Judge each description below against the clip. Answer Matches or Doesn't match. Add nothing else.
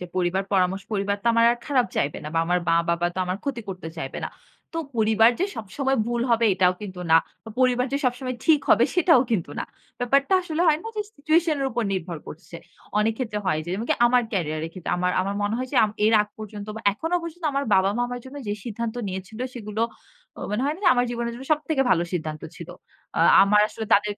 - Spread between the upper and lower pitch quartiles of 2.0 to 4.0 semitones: Doesn't match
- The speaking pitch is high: Matches